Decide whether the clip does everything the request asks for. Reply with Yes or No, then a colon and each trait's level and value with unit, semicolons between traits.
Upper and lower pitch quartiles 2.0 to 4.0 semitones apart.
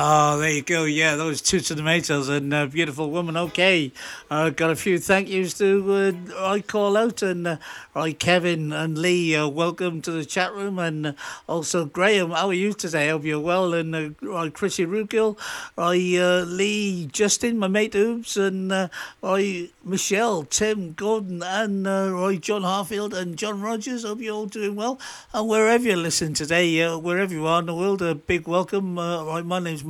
Yes: average, 3.4 semitones